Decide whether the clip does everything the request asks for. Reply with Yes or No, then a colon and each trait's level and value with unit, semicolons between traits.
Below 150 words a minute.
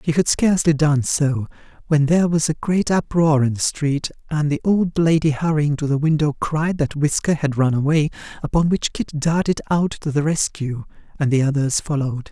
No: average, 195 wpm